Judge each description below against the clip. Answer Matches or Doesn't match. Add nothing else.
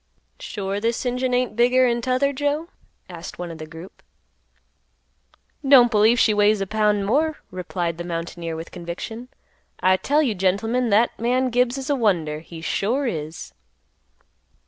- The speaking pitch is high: Matches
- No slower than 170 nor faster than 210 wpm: Doesn't match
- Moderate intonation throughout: Doesn't match